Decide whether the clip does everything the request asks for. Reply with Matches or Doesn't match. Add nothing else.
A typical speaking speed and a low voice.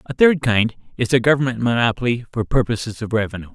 Matches